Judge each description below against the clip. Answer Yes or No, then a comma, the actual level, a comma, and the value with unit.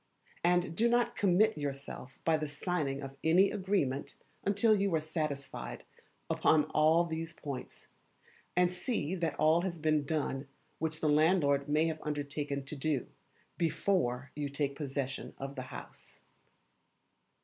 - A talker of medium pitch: Yes, medium, 155 Hz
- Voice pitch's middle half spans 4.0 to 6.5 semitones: No, average, 3.6 semitones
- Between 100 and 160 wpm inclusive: Yes, average, 140 wpm